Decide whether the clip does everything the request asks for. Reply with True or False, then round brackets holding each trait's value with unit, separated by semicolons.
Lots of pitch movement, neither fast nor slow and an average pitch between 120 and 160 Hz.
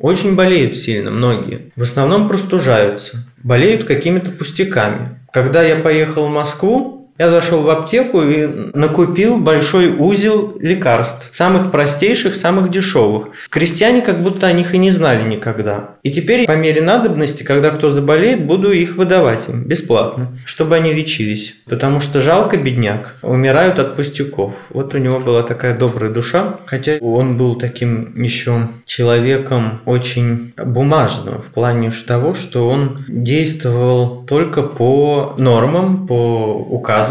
True (6.1 semitones; 140 wpm; 140 Hz)